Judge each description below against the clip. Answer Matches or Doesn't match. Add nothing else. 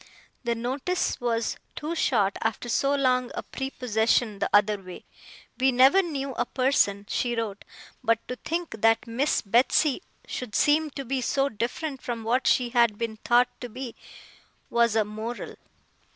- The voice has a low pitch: Doesn't match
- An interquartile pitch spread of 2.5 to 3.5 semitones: Matches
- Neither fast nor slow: Matches